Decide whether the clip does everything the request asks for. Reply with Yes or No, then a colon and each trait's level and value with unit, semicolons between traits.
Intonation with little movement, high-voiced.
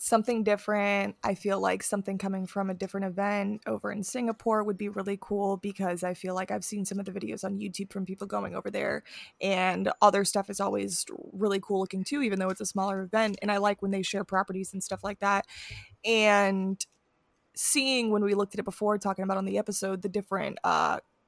Yes: narrow, 1.3 semitones; high, 200 Hz